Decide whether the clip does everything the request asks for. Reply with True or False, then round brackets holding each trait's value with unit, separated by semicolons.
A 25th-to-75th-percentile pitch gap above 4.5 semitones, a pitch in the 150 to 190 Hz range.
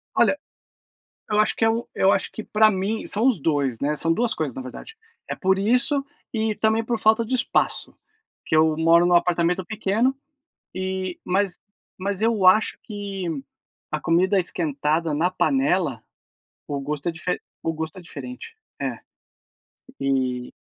True (5.3 semitones; 185 Hz)